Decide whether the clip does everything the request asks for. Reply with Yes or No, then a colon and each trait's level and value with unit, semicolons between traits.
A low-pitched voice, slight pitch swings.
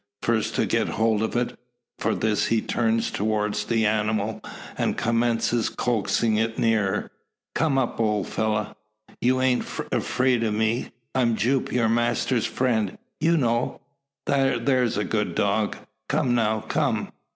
Yes: low, 115 Hz; narrow, 2.2 semitones